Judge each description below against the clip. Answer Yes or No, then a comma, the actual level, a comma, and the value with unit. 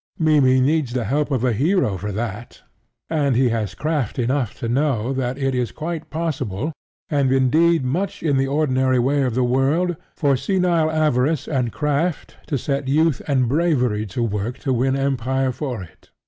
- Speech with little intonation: No, average, 3.8 semitones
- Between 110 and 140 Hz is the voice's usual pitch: Yes, low, 135 Hz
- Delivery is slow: No, average, 175 wpm